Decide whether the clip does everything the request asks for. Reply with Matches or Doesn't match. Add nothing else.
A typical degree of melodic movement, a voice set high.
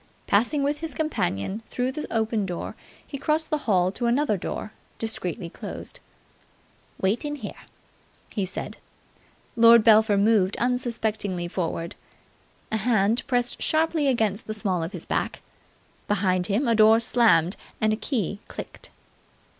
Matches